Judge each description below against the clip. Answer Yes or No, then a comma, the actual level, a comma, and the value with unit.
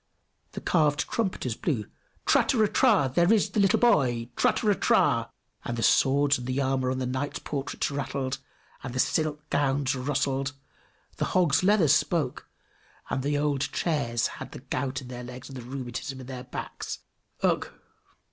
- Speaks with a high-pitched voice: No, low, 135 Hz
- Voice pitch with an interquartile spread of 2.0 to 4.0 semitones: Yes, average, 2.7 semitones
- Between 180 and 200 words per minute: No, average, 150 wpm